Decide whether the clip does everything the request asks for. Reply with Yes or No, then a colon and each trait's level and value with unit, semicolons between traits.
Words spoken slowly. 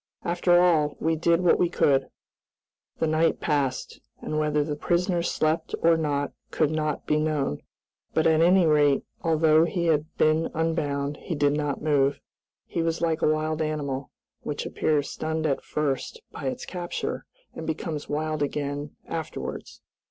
No: average, 160 wpm